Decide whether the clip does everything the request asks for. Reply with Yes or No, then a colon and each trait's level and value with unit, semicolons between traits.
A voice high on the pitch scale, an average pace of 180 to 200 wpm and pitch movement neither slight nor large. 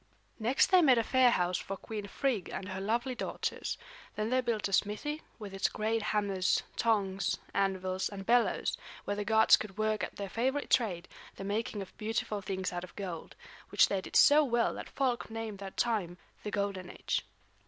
Yes: high, 210 Hz; average, 190 wpm; average, 3.2 semitones